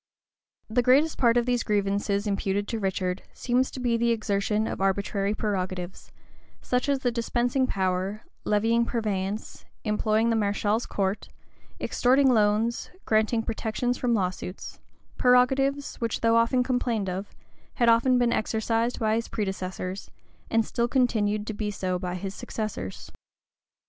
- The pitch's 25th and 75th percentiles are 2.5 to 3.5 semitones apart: Yes, average, 3.2 semitones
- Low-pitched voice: No, high, 220 Hz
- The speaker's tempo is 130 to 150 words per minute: Yes, average, 140 wpm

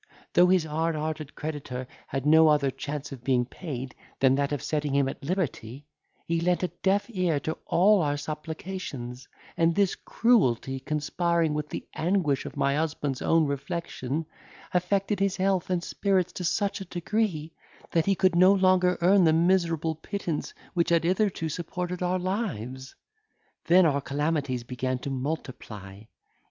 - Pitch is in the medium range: Yes, medium, 160 Hz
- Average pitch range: Yes, average, 4.4 semitones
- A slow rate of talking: No, average, 160 wpm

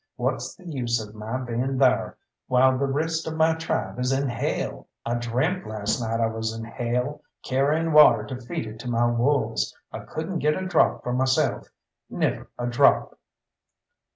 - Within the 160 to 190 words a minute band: Yes, average, 180 wpm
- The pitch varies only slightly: No, average, 4.1 semitones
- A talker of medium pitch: No, low, 125 Hz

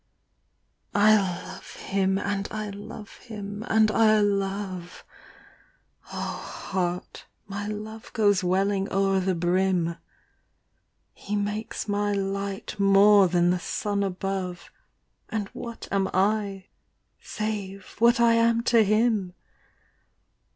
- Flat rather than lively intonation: Yes, narrow, 1.8 semitones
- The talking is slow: Yes, slow, 110 wpm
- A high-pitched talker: Yes, high, 200 Hz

